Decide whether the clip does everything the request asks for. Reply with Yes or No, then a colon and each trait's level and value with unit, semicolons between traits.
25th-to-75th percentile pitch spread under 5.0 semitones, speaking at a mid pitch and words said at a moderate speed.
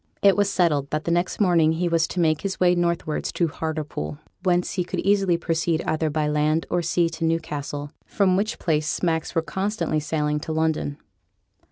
Yes: narrow, 2.6 semitones; medium, 165 Hz; average, 190 wpm